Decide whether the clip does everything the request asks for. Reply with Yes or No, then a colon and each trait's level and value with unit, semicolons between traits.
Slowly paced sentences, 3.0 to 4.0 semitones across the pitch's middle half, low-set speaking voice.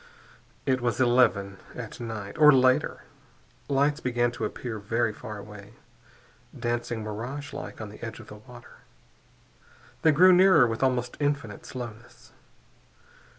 Yes: slow, 130 wpm; average, 3.6 semitones; low, 120 Hz